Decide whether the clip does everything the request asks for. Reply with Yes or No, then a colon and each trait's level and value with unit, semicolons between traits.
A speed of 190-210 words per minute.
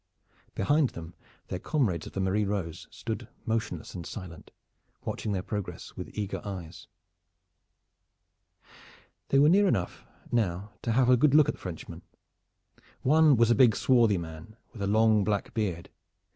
No: average, 155 wpm